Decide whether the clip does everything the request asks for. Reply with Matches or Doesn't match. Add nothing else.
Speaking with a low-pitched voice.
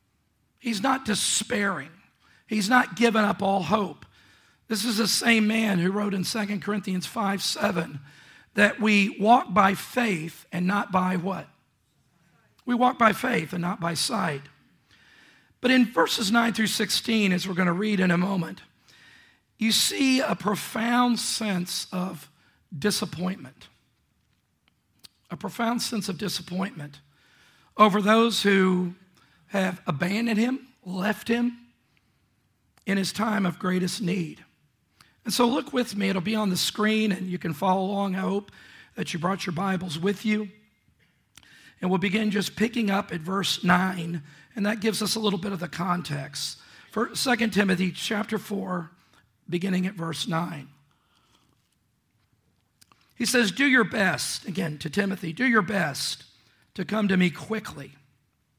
Doesn't match